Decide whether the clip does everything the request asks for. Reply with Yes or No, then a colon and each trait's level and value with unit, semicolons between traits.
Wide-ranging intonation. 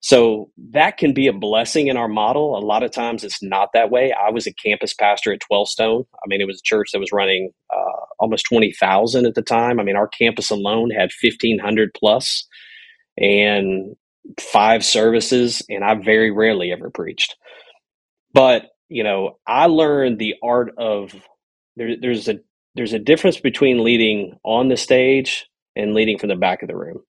No: average, 3.3 semitones